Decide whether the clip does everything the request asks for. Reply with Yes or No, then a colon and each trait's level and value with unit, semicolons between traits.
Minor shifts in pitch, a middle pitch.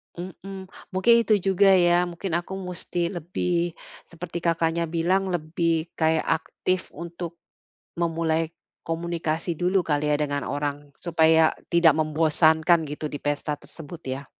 Yes: narrow, 1.8 semitones; medium, 165 Hz